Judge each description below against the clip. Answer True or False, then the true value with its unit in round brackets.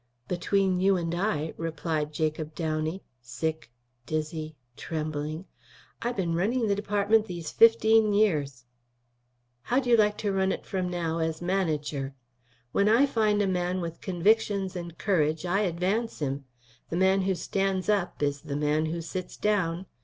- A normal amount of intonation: True (4.3 semitones)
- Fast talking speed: False (155 wpm)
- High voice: False (175 Hz)